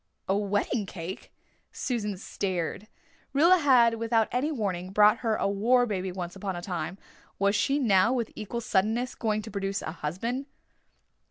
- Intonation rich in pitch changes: No, average, 3.8 semitones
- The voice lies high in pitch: Yes, high, 210 Hz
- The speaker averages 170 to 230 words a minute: No, average, 160 wpm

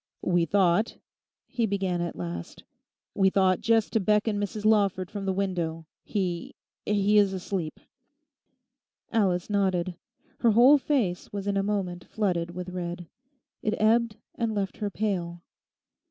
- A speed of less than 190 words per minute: Yes, average, 140 wpm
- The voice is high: Yes, high, 195 Hz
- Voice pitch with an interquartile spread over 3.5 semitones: No, average, 2.9 semitones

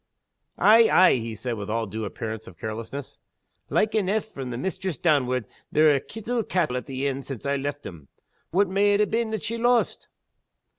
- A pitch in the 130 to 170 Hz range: Yes, medium, 140 Hz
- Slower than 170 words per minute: No, average, 195 wpm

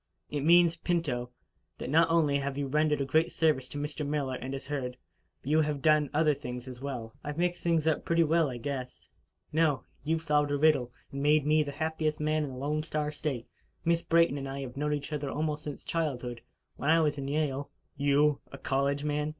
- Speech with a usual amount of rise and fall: No, narrow, 2.2 semitones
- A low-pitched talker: No, medium, 150 Hz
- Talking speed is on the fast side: Yes, fast, 225 wpm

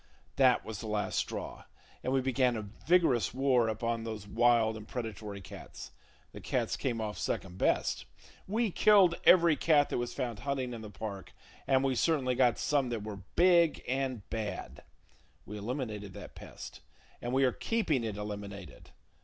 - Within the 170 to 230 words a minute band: Yes, average, 175 wpm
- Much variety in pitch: No, average, 4.1 semitones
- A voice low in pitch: Yes, low, 120 Hz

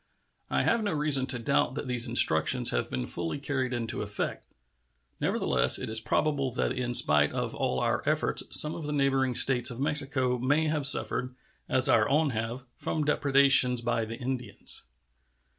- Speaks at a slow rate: No, average, 175 wpm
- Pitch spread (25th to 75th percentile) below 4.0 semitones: Yes, average, 3.2 semitones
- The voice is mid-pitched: No, low, 130 Hz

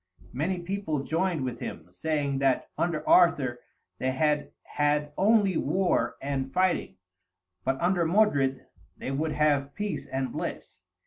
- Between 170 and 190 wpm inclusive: No, slow, 135 wpm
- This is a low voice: No, medium, 150 Hz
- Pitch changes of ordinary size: Yes, average, 4.8 semitones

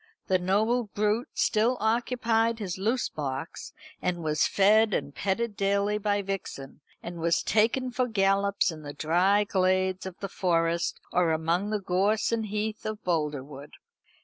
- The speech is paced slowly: No, average, 150 wpm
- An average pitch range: Yes, average, 4.0 semitones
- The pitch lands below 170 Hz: No, high, 195 Hz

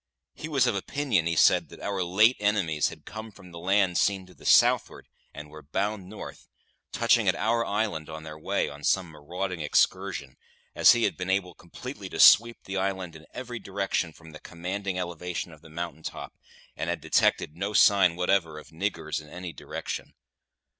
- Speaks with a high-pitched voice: No, very low, 90 Hz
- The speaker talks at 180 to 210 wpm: Yes, average, 190 wpm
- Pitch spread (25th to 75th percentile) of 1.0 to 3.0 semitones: No, average, 3.6 semitones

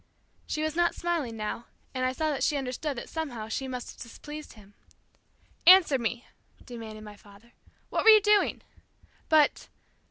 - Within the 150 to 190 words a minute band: Yes, average, 165 wpm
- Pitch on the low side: No, very high, 260 Hz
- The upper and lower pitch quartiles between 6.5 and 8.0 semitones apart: No, wide, 5.4 semitones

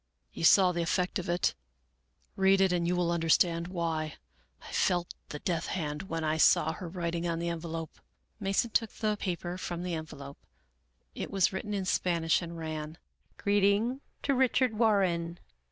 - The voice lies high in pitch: No, medium, 175 Hz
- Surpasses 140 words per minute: Yes, average, 175 wpm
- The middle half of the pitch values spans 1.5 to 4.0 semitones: Yes, average, 2.8 semitones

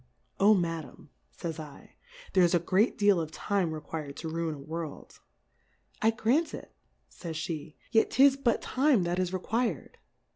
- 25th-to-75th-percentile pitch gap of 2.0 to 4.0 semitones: No, wide, 5.5 semitones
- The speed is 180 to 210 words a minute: No, average, 160 wpm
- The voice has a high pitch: No, medium, 175 Hz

